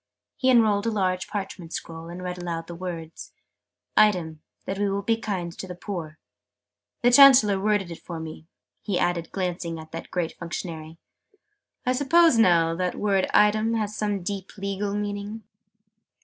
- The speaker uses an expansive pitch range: No, average, 3.6 semitones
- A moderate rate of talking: Yes, average, 165 wpm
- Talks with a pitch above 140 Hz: Yes, high, 190 Hz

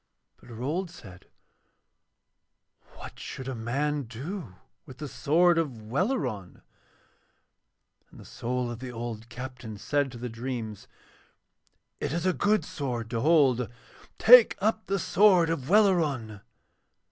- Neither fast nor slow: No, slow, 130 wpm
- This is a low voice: Yes, low, 130 Hz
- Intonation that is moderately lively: No, wide, 6.5 semitones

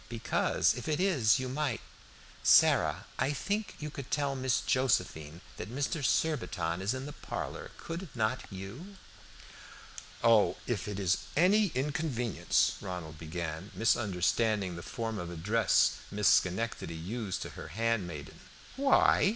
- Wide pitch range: Yes, wide, 7.1 semitones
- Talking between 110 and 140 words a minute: Yes, slow, 135 wpm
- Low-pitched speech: Yes, low, 115 Hz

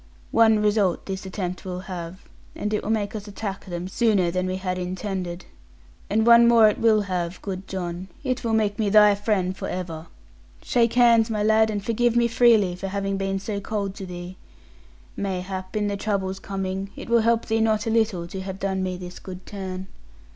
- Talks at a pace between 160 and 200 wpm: Yes, average, 195 wpm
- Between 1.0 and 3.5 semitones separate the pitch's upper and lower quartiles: Yes, average, 2.7 semitones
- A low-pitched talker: No, high, 195 Hz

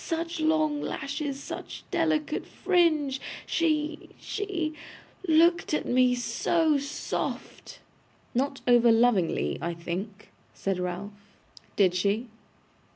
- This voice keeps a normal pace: No, slow, 100 wpm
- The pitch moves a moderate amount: No, wide, 7.1 semitones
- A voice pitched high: Yes, very high, 280 Hz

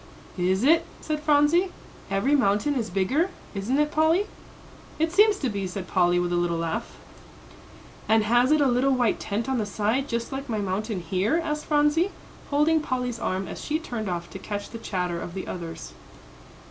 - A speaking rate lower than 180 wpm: No, average, 185 wpm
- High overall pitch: Yes, high, 235 Hz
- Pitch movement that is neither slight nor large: No, wide, 7.5 semitones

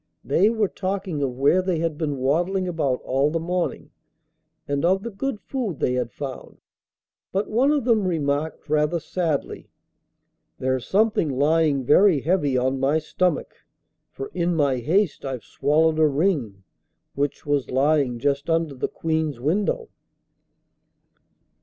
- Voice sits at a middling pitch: Yes, medium, 155 Hz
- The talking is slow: No, average, 145 wpm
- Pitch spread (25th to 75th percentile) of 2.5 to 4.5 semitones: No, average, 4.9 semitones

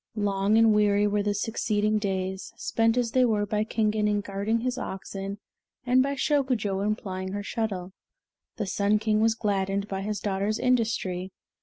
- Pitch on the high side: Yes, high, 210 Hz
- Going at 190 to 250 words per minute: No, average, 170 wpm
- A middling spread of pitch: No, narrow, 2.2 semitones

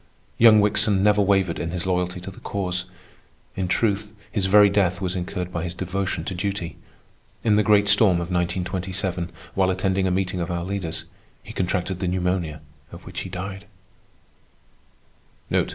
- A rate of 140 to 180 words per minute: Yes, average, 165 wpm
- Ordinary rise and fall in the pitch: No, narrow, 1.9 semitones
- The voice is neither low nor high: No, very low, 95 Hz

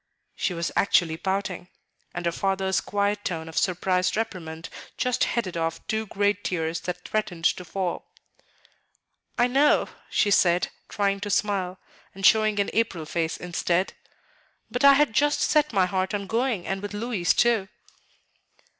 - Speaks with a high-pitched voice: Yes, high, 195 Hz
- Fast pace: No, average, 155 wpm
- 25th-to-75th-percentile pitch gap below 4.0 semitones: Yes, average, 3.4 semitones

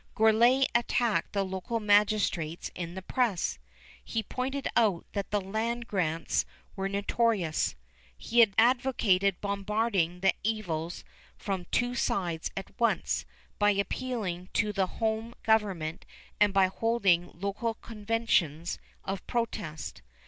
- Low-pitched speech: No, high, 205 Hz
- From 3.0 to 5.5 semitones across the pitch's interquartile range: Yes, average, 3.8 semitones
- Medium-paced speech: No, slow, 120 wpm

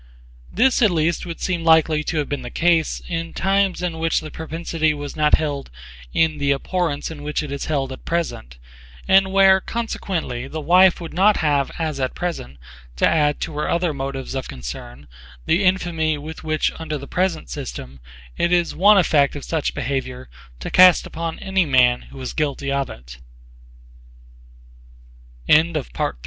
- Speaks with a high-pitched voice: No, medium, 160 Hz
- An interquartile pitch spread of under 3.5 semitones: No, average, 3.8 semitones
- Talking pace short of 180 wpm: Yes, average, 165 wpm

